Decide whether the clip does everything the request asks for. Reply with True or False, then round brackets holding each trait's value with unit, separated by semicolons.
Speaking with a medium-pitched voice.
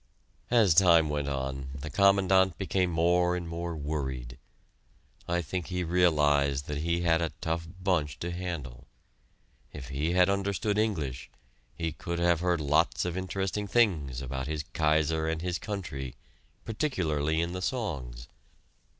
False (85 Hz)